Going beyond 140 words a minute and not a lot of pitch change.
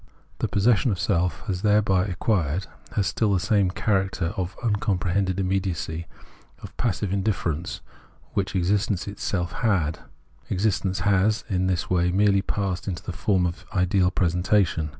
Yes: average, 150 wpm; narrow, 2.2 semitones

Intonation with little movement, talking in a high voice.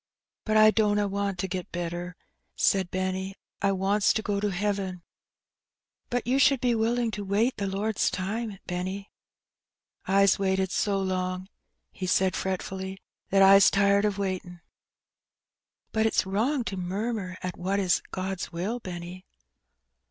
Yes: narrow, 1.9 semitones; high, 195 Hz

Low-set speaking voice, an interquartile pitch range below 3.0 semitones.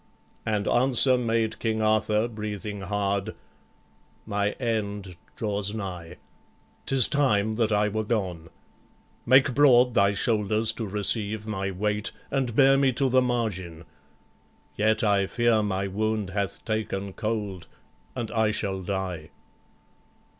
Yes: low, 105 Hz; narrow, 2.4 semitones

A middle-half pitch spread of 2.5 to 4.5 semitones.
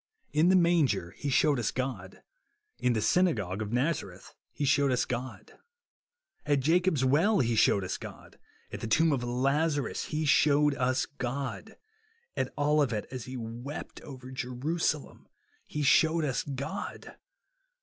Yes: average, 3.5 semitones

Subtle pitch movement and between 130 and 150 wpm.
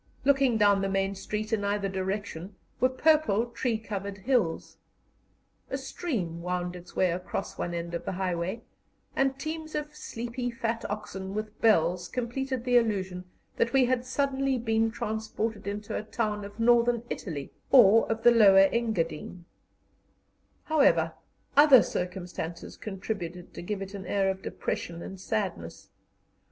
No: average, 4.1 semitones; average, 145 wpm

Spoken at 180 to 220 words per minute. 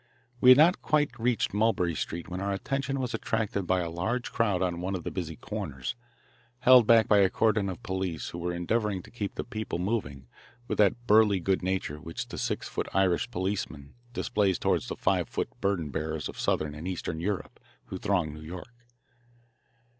Yes: average, 190 wpm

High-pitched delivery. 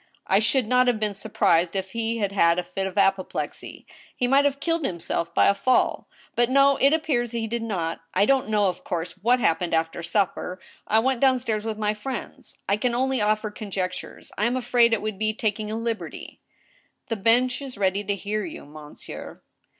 Yes: high, 215 Hz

